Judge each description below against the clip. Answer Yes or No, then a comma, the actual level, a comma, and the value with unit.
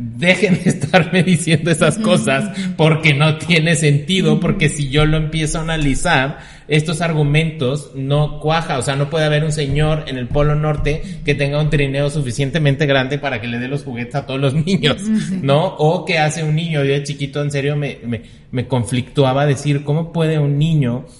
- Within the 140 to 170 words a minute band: No, fast, 190 wpm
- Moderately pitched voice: Yes, medium, 150 Hz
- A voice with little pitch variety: Yes, narrow, 2.3 semitones